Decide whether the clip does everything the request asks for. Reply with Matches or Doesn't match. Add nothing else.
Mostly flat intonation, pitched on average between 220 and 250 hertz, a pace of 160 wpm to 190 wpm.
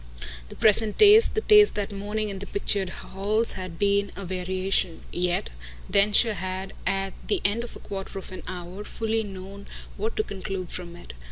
Doesn't match